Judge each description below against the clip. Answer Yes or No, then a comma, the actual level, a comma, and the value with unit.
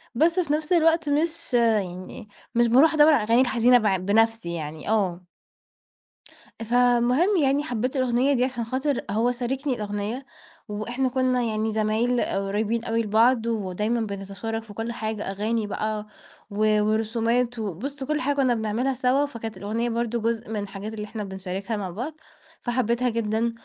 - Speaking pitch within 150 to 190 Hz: No, high, 230 Hz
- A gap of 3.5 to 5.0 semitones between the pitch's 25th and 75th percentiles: No, average, 3.0 semitones